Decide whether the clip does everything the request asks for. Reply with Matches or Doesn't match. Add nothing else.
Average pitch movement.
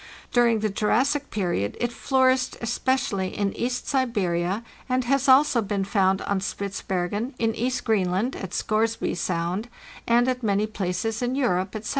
Matches